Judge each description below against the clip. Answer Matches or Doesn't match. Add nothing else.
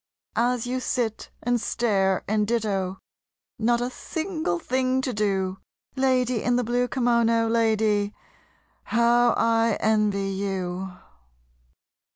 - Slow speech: Matches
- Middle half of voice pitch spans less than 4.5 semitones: Matches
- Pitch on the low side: Doesn't match